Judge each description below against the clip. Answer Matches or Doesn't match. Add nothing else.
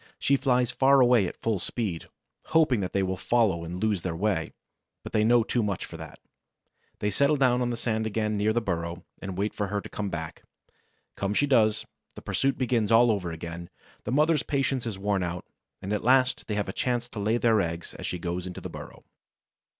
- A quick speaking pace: Matches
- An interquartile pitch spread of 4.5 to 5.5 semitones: Matches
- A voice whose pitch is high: Doesn't match